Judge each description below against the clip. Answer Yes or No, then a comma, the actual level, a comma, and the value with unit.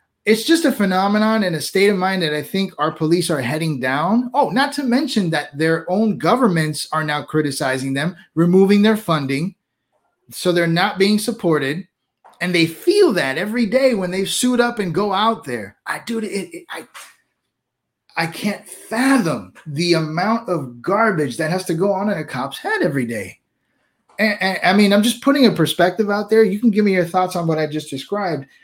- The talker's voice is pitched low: No, high, 190 Hz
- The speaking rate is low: No, average, 200 wpm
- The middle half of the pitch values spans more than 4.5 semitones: Yes, wide, 5.5 semitones